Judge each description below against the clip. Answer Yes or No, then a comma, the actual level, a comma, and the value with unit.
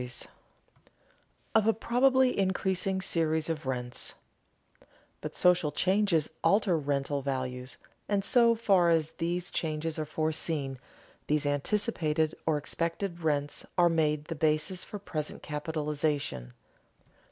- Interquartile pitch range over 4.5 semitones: No, average, 4.1 semitones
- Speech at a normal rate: No, slow, 120 wpm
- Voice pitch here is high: No, medium, 160 Hz